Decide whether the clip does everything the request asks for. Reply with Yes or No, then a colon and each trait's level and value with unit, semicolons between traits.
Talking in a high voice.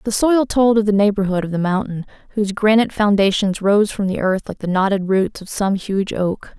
Yes: high, 200 Hz